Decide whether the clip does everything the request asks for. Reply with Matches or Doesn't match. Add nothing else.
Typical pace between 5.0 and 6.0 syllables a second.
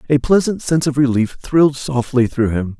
Matches